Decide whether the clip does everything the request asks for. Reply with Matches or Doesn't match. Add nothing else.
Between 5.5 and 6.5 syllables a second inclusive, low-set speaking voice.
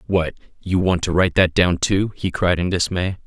Doesn't match